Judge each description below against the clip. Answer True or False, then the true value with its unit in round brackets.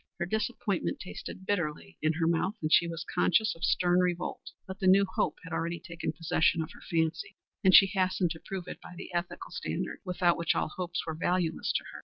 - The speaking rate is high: True (215 wpm)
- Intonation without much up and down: True (2.2 semitones)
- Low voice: False (175 Hz)